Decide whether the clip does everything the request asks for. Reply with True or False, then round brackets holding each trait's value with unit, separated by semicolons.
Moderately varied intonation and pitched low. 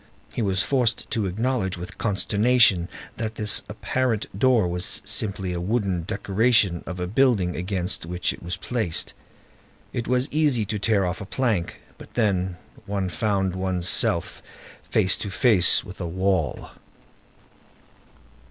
True (3.8 semitones; 100 Hz)